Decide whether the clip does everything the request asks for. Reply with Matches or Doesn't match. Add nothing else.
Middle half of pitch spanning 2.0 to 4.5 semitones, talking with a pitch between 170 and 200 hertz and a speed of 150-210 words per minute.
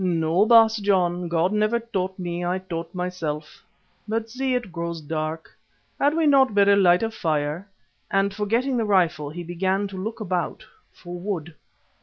Matches